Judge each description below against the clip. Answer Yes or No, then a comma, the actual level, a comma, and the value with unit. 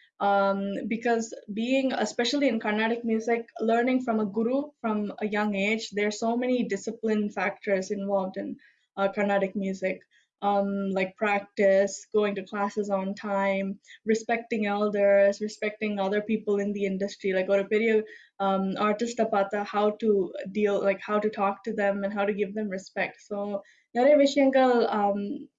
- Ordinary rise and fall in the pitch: No, narrow, 2.0 semitones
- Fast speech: Yes, fast, 150 wpm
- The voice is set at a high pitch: Yes, high, 205 Hz